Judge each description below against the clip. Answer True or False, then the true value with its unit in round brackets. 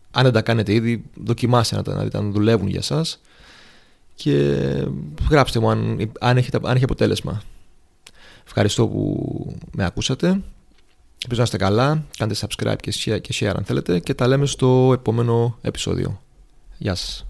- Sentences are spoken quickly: False (155 wpm)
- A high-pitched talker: False (115 Hz)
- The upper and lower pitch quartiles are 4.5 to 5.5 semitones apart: False (4.0 semitones)